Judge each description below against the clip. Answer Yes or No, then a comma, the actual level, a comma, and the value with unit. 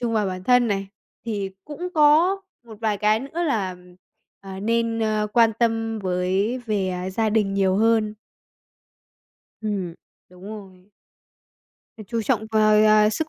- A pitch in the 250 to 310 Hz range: No, high, 215 Hz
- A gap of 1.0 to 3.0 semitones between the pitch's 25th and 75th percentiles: Yes, average, 2.7 semitones